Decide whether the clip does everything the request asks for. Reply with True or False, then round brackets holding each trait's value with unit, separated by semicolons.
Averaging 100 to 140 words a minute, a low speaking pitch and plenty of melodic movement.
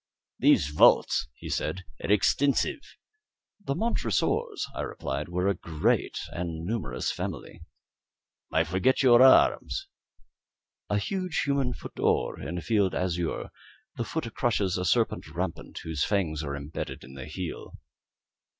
True (135 wpm; 95 Hz; 6.6 semitones)